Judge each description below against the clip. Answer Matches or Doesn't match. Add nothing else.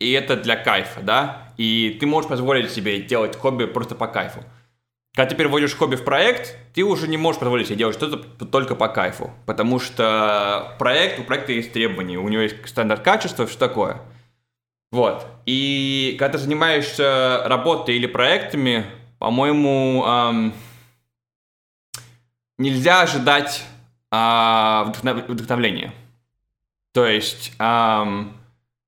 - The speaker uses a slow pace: Doesn't match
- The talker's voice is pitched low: Matches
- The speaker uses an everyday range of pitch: Matches